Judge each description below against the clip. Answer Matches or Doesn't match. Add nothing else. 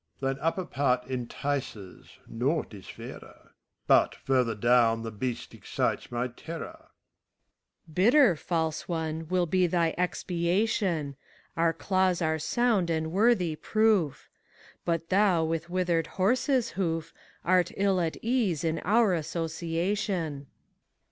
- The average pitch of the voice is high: Doesn't match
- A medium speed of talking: Doesn't match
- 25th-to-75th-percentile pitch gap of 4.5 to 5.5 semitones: Doesn't match